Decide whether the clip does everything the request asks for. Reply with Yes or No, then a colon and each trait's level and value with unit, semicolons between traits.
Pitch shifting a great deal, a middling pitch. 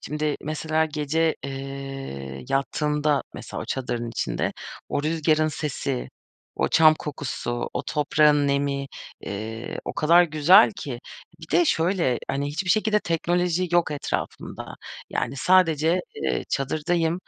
No: average, 3.1 semitones; medium, 150 Hz